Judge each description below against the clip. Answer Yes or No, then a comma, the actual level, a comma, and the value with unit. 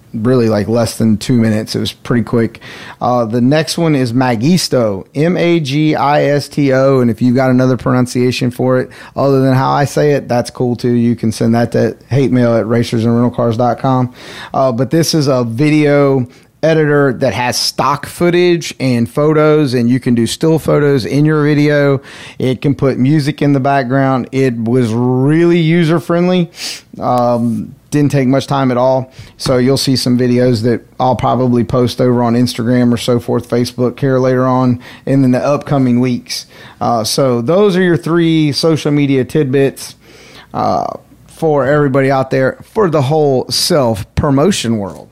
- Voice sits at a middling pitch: No, low, 130 Hz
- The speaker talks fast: No, average, 180 wpm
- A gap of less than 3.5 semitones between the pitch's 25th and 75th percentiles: Yes, average, 3.0 semitones